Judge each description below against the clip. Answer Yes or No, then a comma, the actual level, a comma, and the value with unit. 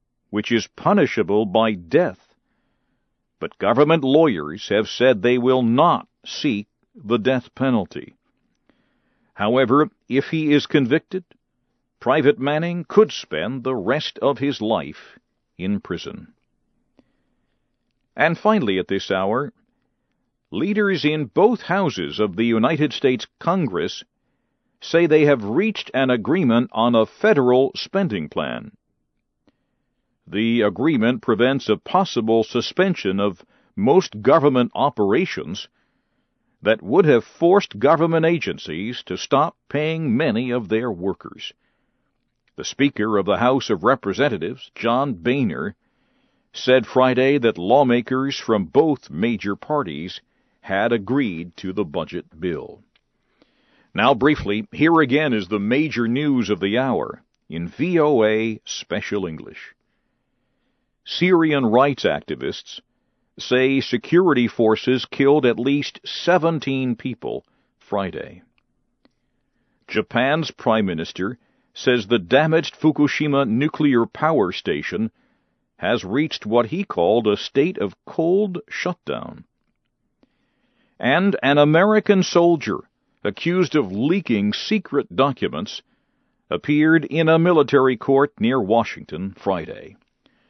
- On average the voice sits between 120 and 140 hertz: Yes, low, 135 Hz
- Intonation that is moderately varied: No, wide, 6.0 semitones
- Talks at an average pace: No, slow, 110 wpm